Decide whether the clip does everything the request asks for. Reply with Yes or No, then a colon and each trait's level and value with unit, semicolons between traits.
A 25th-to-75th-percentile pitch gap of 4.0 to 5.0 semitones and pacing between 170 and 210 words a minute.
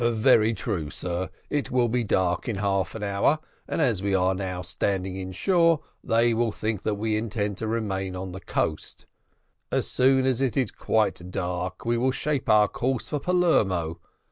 Yes: average, 4.3 semitones; average, 180 wpm